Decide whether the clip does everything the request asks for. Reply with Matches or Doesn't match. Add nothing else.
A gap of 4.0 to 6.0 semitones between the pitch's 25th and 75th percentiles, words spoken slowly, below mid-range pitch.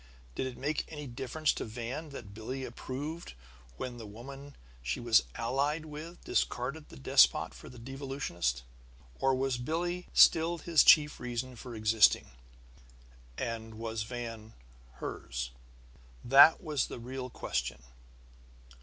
Matches